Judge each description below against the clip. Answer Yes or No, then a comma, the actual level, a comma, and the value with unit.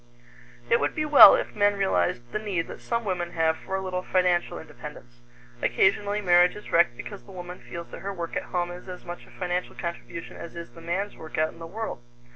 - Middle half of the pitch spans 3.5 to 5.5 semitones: No, average, 2.7 semitones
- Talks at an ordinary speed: No, fast, 225 wpm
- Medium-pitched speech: Yes, medium, 180 Hz